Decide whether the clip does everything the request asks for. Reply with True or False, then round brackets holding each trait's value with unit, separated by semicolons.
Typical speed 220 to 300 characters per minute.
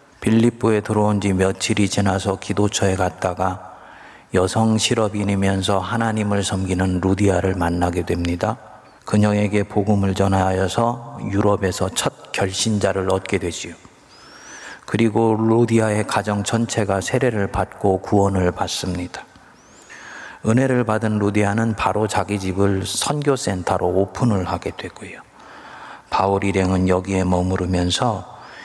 True (285 characters per minute)